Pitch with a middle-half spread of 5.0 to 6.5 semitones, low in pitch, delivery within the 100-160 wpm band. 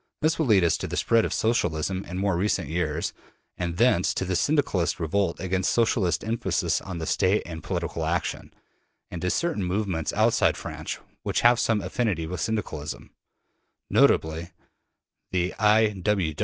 No: average, 4.4 semitones; very low, 95 Hz; average, 155 wpm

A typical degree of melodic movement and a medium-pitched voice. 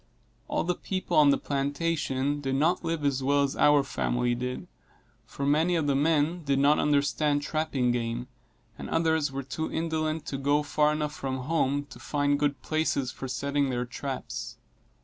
No: narrow, 2.3 semitones; medium, 145 Hz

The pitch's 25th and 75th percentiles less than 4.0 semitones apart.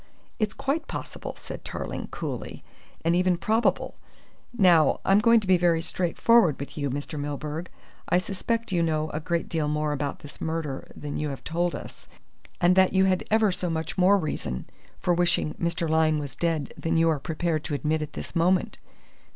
Yes: average, 3.2 semitones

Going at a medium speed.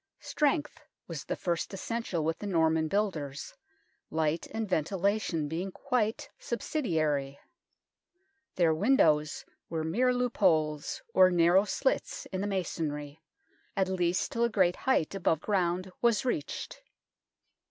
No: slow, 125 wpm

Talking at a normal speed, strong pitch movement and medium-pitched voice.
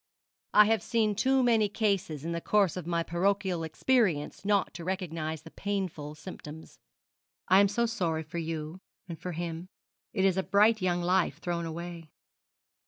No: average, 170 wpm; average, 3.6 semitones; medium, 180 Hz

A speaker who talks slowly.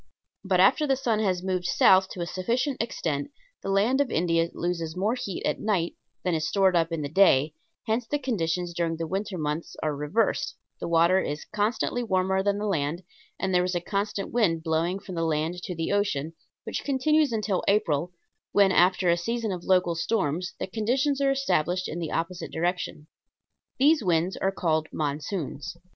No: average, 185 wpm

